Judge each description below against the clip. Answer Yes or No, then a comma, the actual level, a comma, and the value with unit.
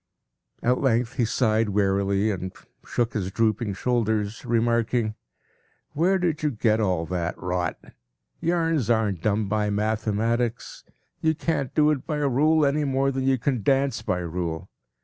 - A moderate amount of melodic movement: Yes, average, 4.6 semitones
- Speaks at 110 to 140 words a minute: No, average, 150 wpm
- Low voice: Yes, low, 115 Hz